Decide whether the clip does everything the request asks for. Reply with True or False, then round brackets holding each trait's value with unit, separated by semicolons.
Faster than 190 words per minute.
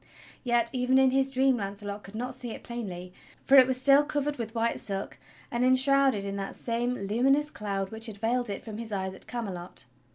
True (205 wpm)